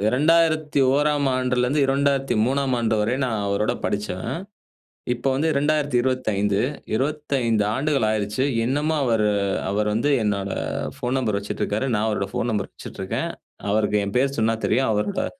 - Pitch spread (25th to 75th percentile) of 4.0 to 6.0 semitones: Yes, average, 4.8 semitones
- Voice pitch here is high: No, low, 125 Hz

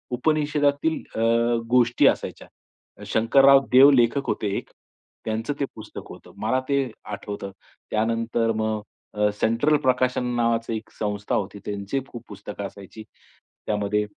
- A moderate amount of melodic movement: Yes, average, 3.8 semitones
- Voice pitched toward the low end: Yes, low, 115 Hz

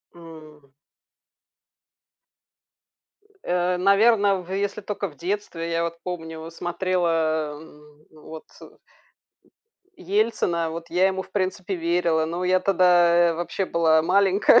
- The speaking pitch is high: No, medium, 175 Hz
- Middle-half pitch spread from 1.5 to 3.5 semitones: Yes, narrow, 2.5 semitones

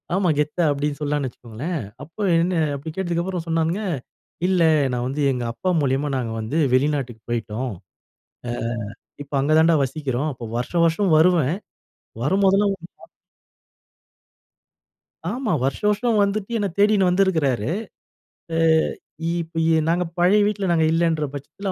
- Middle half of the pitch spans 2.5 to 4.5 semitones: No, average, 5.2 semitones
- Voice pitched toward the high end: No, medium, 165 Hz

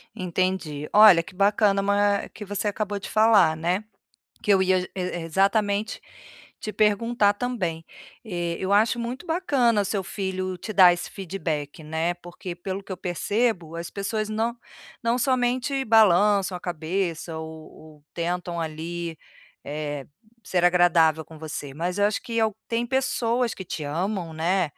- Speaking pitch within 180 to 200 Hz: Yes, high, 190 Hz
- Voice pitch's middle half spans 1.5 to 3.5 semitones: No, average, 4.0 semitones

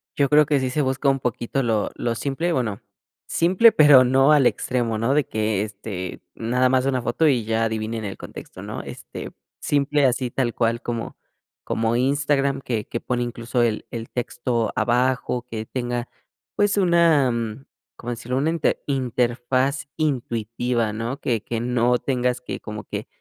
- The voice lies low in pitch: Yes, low, 125 Hz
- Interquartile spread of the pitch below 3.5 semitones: Yes, average, 2.8 semitones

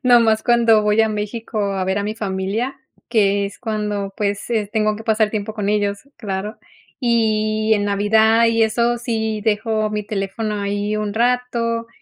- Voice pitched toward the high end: Yes, high, 215 Hz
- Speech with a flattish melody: Yes, narrow, 1.8 semitones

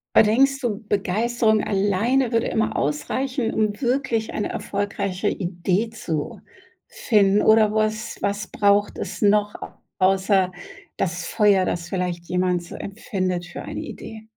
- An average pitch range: Yes, average, 3.1 semitones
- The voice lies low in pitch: No, high, 205 Hz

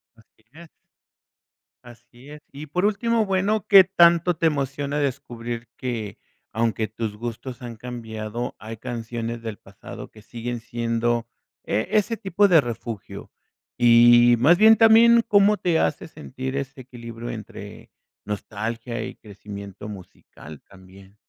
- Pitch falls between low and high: No, low, 120 Hz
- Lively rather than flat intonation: Yes, wide, 6.2 semitones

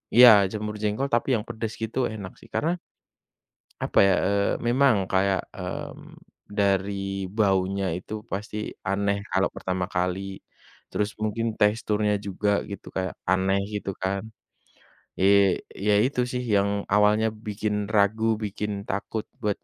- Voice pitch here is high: No, low, 100 Hz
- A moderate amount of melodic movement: No, narrow, 1.7 semitones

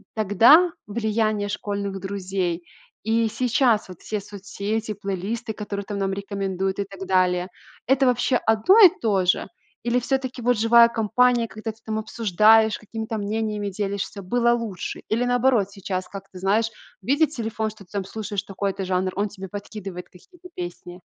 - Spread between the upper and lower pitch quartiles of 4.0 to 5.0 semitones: No, average, 2.8 semitones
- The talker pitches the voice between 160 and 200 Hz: No, high, 210 Hz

